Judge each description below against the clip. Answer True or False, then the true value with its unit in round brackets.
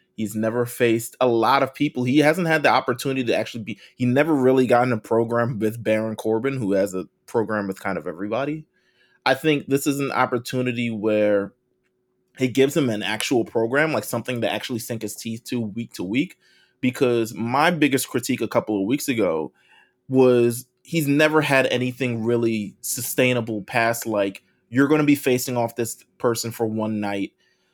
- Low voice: True (120 Hz)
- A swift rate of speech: False (185 wpm)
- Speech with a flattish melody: False (3.0 semitones)